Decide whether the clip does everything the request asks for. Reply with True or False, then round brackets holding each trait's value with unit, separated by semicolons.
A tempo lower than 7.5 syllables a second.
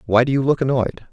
False (7.9 syllables/s)